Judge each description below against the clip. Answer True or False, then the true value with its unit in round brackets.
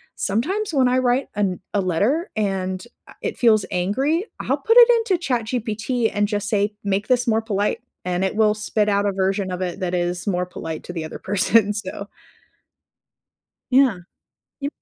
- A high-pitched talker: True (210 Hz)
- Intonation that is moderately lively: True (4.5 semitones)